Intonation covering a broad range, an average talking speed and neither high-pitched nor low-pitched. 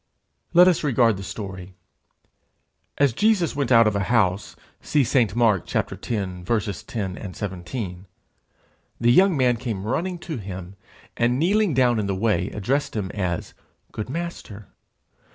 No: wide, 6.1 semitones; average, 145 wpm; low, 115 Hz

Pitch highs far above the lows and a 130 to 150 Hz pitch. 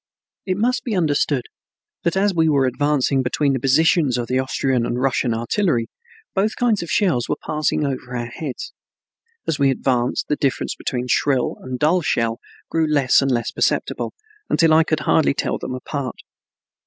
No: average, 4.3 semitones; medium, 140 Hz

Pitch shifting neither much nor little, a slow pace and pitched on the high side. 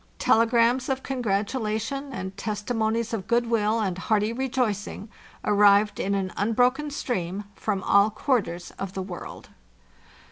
Yes: average, 3.1 semitones; slow, 120 wpm; high, 215 Hz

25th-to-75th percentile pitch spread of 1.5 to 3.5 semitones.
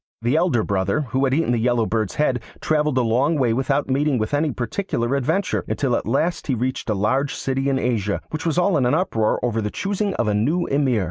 No: average, 4.5 semitones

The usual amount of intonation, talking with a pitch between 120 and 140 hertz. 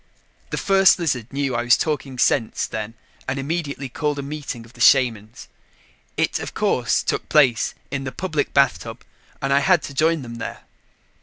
Yes: average, 3.8 semitones; low, 135 Hz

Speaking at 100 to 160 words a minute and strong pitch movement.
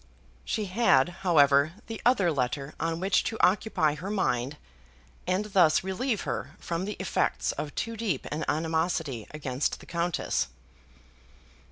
No: average, 140 wpm; average, 4.9 semitones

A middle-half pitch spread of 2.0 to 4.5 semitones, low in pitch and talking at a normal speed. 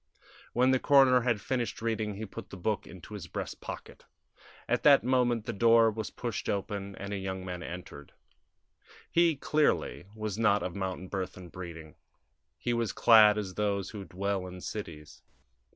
Yes: average, 3.8 semitones; low, 105 Hz; average, 170 wpm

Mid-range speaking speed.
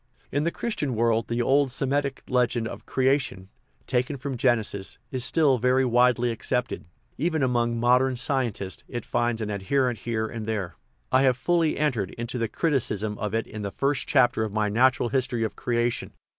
Yes: average, 185 wpm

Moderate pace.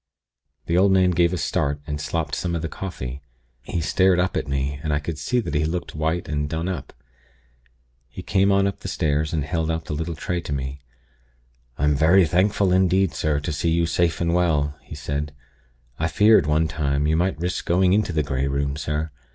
No: fast, 210 wpm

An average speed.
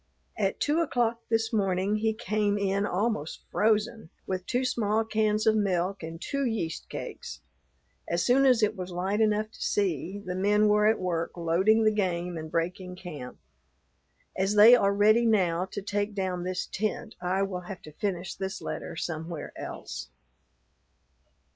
Yes: average, 165 wpm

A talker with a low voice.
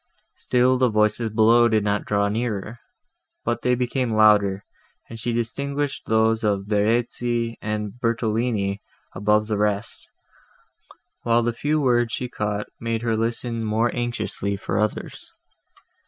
Yes: low, 115 Hz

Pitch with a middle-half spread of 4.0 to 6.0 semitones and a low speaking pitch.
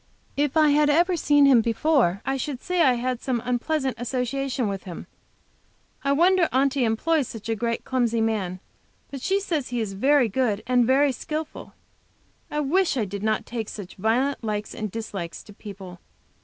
No: average, 4.7 semitones; very high, 250 Hz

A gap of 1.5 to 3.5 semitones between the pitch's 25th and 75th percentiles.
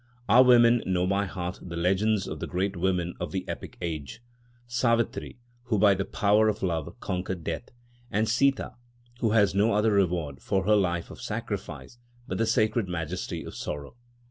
No: average, 4.1 semitones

